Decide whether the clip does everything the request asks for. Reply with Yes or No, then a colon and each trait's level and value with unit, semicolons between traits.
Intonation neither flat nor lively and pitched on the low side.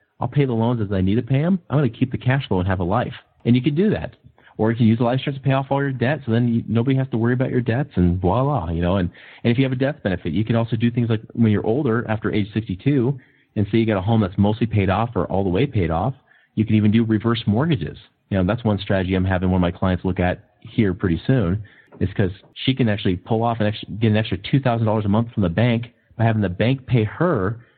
Yes: average, 3.8 semitones; low, 115 Hz